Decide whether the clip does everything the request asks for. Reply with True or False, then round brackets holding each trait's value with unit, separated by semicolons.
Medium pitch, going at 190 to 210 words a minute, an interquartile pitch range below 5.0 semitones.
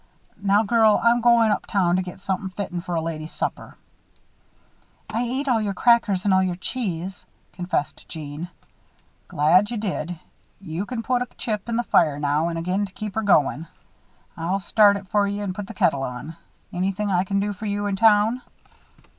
False (195 Hz; 195 wpm; 3.4 semitones)